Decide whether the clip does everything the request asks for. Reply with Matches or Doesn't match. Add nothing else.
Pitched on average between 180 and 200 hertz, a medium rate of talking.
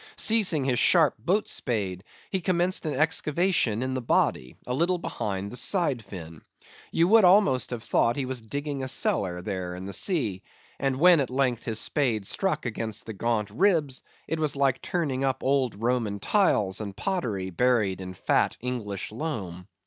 Doesn't match